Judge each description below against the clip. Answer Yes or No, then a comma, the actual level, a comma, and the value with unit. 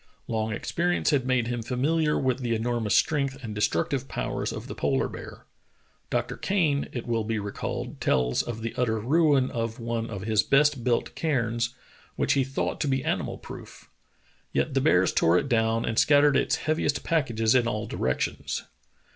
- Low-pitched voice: Yes, low, 120 Hz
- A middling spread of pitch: Yes, average, 3.7 semitones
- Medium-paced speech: Yes, average, 180 wpm